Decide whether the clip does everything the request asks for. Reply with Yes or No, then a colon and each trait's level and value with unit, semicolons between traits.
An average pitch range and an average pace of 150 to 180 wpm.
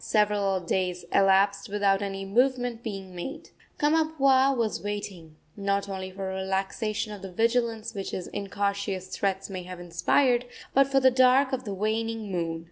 Yes: average, 3.9 semitones; average, 160 wpm